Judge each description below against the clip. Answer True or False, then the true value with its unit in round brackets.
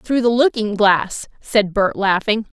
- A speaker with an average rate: True (160 wpm)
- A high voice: True (215 Hz)